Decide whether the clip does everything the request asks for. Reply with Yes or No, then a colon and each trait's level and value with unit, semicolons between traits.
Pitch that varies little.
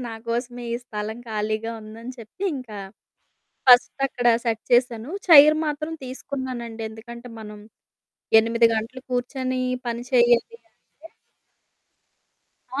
Yes: narrow, 2.3 semitones